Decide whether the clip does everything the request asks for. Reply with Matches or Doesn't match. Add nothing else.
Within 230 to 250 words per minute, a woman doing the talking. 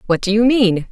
Doesn't match